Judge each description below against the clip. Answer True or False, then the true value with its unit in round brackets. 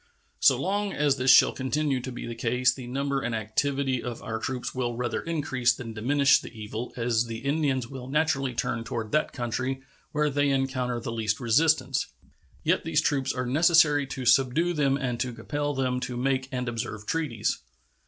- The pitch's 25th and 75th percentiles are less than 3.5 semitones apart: True (3.0 semitones)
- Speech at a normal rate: True (185 wpm)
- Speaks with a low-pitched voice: True (130 Hz)